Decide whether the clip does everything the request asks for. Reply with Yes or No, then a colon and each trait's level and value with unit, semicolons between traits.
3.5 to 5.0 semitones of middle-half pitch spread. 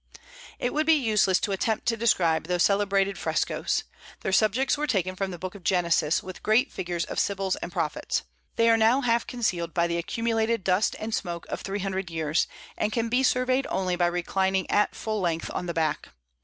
Yes: average, 4.3 semitones